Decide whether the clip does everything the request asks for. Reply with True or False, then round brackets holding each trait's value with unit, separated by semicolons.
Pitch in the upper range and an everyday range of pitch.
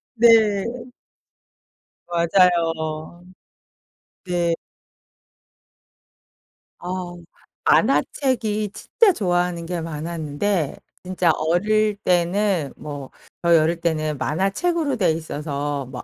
False (175 Hz; 3.6 semitones)